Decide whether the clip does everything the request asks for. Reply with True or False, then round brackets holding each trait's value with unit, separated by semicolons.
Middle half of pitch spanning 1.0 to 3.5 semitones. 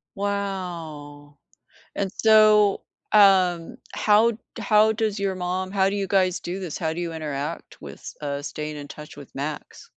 False (4.7 semitones)